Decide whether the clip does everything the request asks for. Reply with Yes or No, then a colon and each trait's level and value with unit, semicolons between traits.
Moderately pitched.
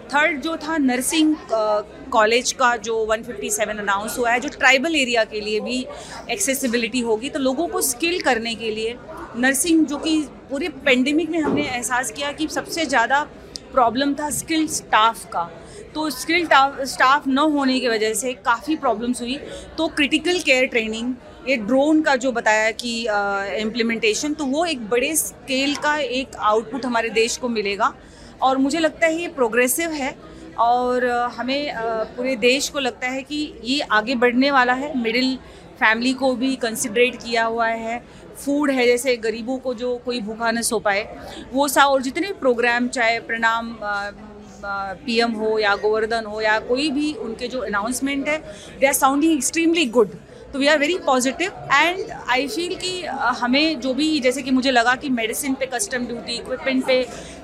No: very high, 255 Hz